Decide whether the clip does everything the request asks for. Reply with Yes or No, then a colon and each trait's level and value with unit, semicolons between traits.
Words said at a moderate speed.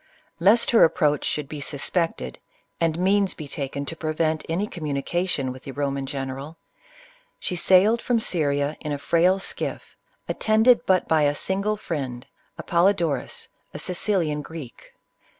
Yes: average, 150 wpm